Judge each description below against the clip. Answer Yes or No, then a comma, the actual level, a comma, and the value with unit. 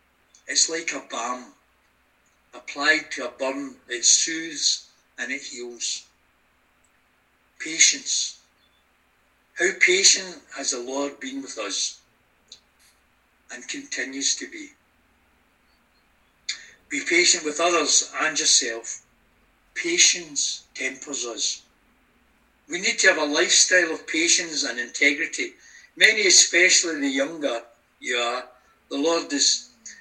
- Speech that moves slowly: Yes, slow, 110 wpm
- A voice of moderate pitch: Yes, medium, 160 Hz